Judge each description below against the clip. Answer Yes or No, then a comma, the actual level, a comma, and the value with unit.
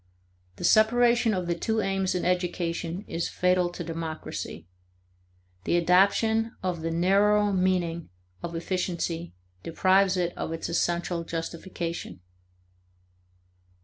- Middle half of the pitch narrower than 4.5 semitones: Yes, narrow, 2.5 semitones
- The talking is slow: Yes, slow, 115 wpm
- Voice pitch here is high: No, medium, 180 Hz